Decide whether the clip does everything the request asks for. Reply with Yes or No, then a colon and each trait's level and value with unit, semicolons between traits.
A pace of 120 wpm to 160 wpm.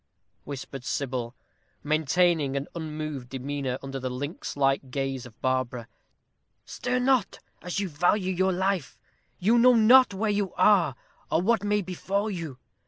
Yes: average, 145 wpm